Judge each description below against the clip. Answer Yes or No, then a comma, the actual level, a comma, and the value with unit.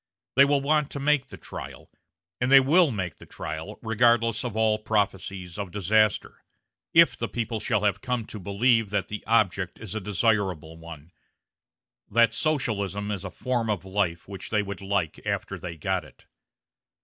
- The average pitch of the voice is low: Yes, low, 105 Hz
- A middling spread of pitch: Yes, average, 3.4 semitones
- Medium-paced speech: Yes, average, 175 wpm